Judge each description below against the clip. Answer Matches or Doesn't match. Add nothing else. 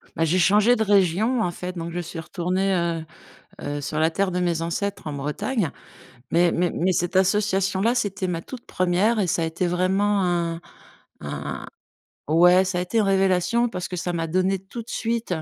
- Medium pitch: Matches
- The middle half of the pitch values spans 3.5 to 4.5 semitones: Doesn't match